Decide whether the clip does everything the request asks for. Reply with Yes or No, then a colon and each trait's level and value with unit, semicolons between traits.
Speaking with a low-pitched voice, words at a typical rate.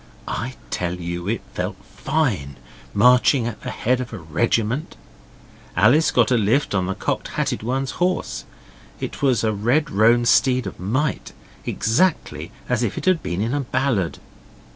Yes: low, 120 Hz; average, 165 wpm